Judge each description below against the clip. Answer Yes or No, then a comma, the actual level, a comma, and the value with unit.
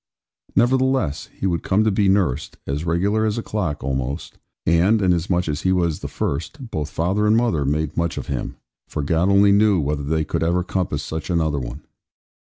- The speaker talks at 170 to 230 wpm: Yes, average, 195 wpm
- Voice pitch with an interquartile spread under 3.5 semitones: No, average, 5.0 semitones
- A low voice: Yes, very low, 85 Hz